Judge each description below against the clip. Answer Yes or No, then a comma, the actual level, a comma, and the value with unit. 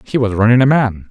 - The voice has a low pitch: Yes, low, 115 Hz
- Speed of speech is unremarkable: No, fast, 270 wpm